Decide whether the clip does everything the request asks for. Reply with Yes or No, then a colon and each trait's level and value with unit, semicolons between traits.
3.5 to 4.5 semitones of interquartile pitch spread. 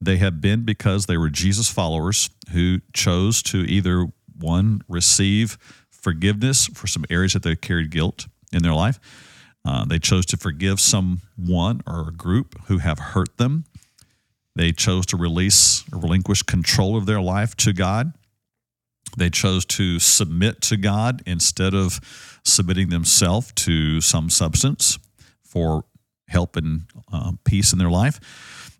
Yes: average, 3.8 semitones